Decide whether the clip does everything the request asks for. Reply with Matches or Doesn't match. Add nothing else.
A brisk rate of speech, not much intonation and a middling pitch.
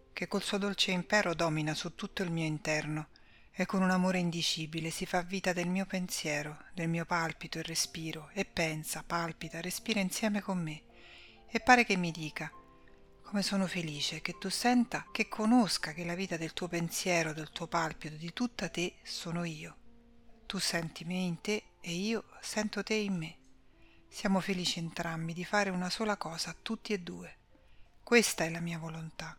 Doesn't match